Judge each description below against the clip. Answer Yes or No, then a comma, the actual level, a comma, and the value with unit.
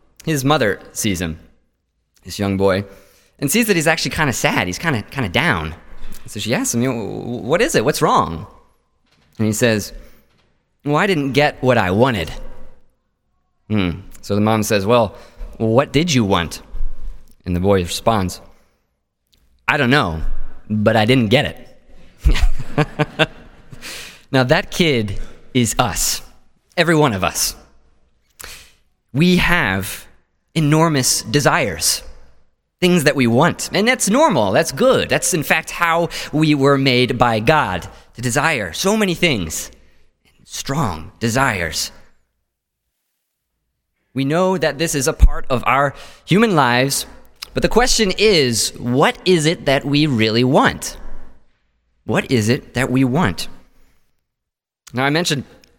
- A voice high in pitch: No, low, 125 Hz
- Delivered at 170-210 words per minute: No, average, 140 wpm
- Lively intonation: Yes, wide, 7.8 semitones